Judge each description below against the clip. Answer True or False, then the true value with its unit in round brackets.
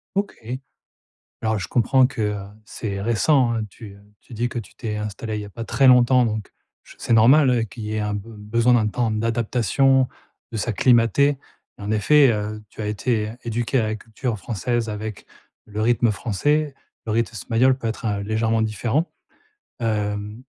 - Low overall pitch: True (115 Hz)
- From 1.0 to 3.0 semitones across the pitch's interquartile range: True (2.5 semitones)